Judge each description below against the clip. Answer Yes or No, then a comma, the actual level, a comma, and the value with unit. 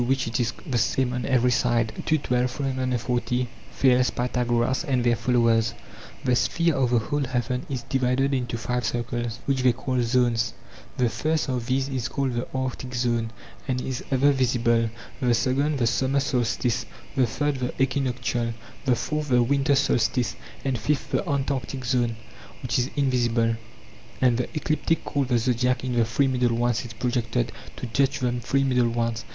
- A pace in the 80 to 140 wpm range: No, average, 175 wpm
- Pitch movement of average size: No, narrow, 1.9 semitones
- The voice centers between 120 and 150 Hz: Yes, low, 125 Hz